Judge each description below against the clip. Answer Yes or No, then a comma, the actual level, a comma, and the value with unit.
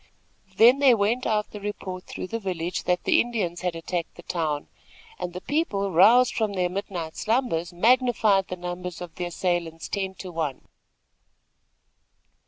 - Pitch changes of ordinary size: Yes, average, 3.7 semitones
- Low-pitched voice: No, medium, 185 Hz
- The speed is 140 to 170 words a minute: Yes, average, 160 wpm